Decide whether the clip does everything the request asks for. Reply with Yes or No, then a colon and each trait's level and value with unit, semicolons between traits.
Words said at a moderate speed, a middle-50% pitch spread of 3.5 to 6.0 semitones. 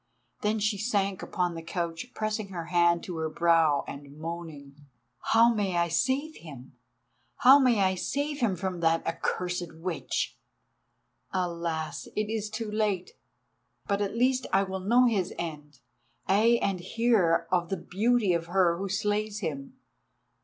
Yes: average, 150 wpm; average, 4.2 semitones